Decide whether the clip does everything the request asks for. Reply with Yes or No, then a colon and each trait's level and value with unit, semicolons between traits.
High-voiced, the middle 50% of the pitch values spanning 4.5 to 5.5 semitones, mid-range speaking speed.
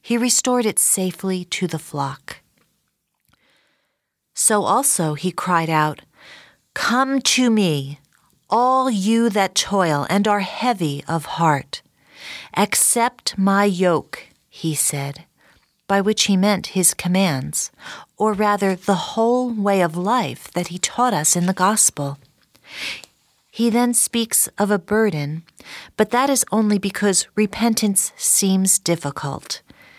No: high, 195 Hz; average, 4.8 semitones; slow, 125 wpm